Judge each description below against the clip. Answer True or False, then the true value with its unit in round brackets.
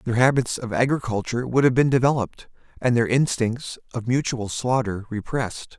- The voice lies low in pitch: True (120 Hz)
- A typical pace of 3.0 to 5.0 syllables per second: False (5.4 syllables/s)